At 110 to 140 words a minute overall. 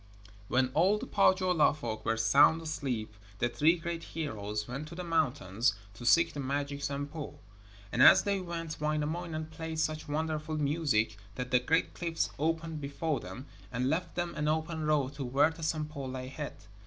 No: average, 175 wpm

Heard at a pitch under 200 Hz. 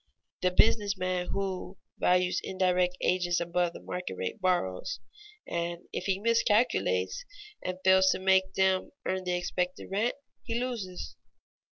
Yes: medium, 185 Hz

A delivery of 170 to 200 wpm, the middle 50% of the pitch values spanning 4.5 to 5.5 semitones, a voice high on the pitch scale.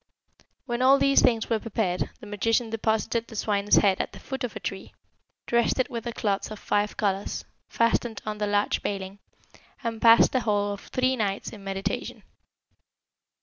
No: average, 180 wpm; narrow, 2.5 semitones; high, 220 Hz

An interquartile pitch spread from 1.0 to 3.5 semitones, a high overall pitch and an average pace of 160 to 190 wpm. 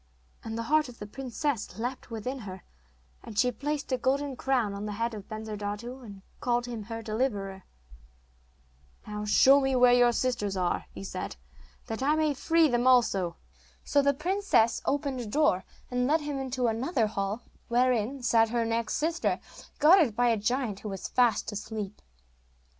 No: average, 4.0 semitones; high, 240 Hz; average, 170 wpm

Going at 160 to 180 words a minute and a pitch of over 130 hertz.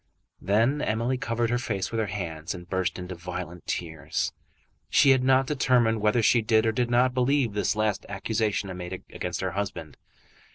No: average, 175 wpm; low, 110 Hz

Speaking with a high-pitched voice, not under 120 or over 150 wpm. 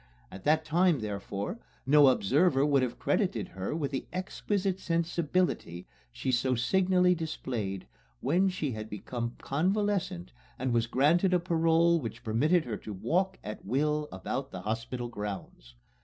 No: medium, 140 Hz; average, 145 wpm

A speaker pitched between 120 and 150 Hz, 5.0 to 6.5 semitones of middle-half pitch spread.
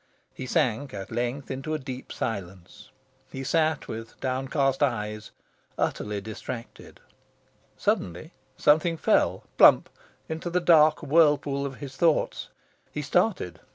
Yes: low, 135 Hz; average, 5.3 semitones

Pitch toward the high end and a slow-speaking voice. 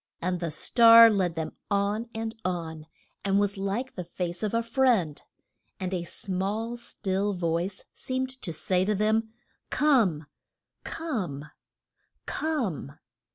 Yes: high, 200 Hz; slow, 130 wpm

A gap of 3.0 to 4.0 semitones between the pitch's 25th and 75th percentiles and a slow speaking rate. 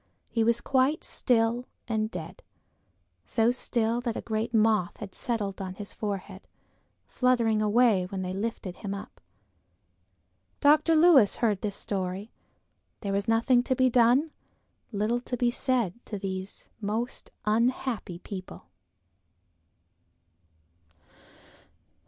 Yes: average, 3.4 semitones; slow, 120 wpm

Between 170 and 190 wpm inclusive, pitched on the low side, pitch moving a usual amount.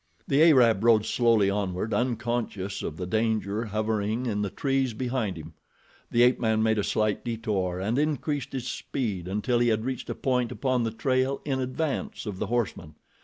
Yes: average, 180 wpm; low, 115 Hz; average, 3.5 semitones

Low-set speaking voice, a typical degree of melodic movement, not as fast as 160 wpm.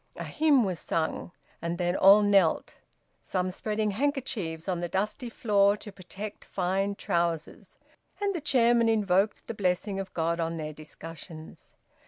No: high, 195 Hz; average, 3.9 semitones; average, 150 wpm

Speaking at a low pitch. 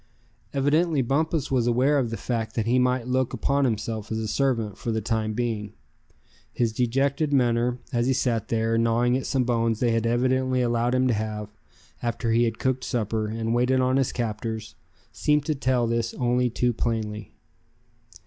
Yes: low, 120 Hz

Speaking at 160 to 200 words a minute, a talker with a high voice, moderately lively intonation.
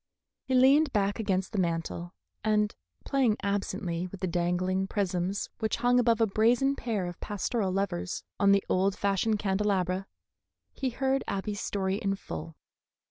No: average, 150 wpm; high, 200 Hz; average, 3.2 semitones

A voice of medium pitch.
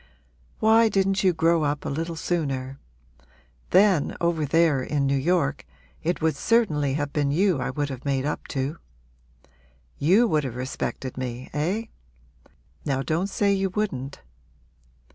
Yes: medium, 155 Hz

